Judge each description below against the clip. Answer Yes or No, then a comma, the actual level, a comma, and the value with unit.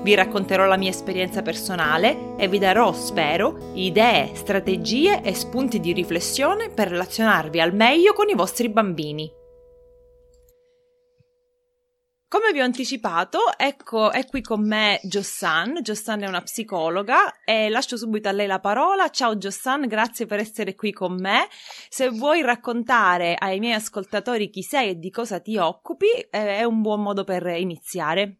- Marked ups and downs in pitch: Yes, wide, 5.8 semitones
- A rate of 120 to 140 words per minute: No, average, 150 wpm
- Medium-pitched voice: No, high, 220 Hz